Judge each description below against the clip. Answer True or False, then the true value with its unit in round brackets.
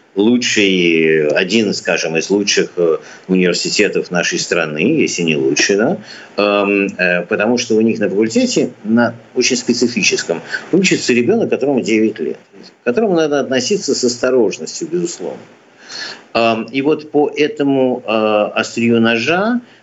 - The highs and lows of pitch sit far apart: True (5.7 semitones)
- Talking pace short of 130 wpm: True (120 wpm)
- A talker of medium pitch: False (120 Hz)